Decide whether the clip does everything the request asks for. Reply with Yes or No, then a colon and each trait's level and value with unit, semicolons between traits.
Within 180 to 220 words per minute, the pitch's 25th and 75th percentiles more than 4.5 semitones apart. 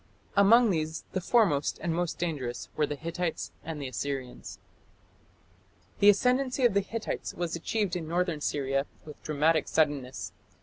No: average, 145 wpm; average, 5.1 semitones